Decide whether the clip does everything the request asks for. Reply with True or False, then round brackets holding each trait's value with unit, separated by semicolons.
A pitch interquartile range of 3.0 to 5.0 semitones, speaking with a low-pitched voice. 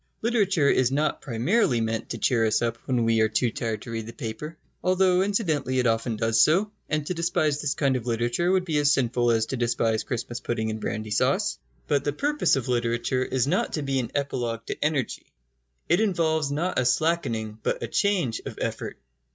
False (5.4 semitones; 130 Hz)